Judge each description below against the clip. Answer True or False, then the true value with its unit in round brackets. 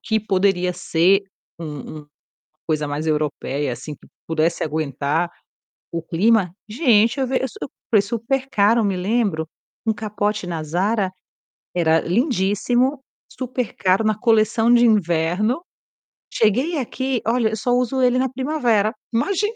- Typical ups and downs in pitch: False (6.1 semitones)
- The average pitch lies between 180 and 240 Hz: True (210 Hz)